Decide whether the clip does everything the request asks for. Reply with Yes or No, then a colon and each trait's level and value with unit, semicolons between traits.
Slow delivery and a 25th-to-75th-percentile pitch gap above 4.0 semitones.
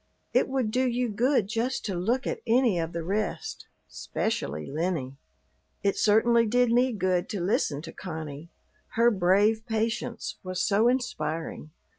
No: average, 150 wpm; wide, 5.4 semitones